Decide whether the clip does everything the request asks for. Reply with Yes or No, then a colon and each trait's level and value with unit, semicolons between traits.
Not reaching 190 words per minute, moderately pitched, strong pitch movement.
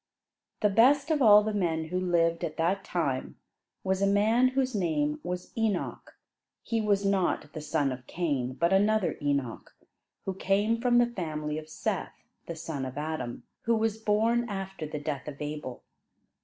Yes: average, 170 wpm; medium, 180 Hz; wide, 5.9 semitones